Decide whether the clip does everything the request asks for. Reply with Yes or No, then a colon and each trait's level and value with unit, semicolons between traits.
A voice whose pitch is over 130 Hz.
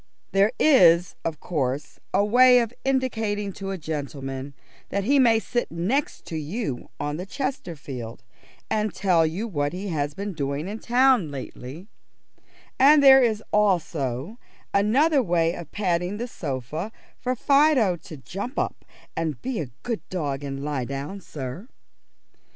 Yes: medium, 185 Hz